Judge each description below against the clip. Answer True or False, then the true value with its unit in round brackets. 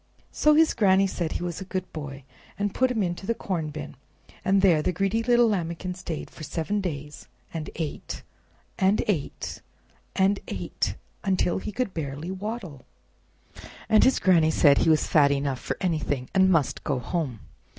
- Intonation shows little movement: False (4.3 semitones)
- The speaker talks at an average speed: True (170 wpm)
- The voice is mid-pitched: True (180 Hz)